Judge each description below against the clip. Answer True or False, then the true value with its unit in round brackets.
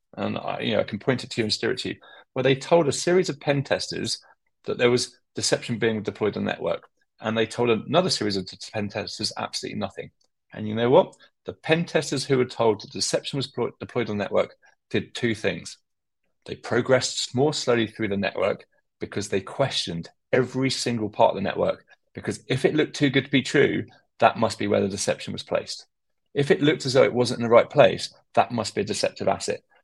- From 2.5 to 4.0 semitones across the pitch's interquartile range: True (3.6 semitones)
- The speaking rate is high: True (230 wpm)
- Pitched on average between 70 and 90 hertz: False (120 Hz)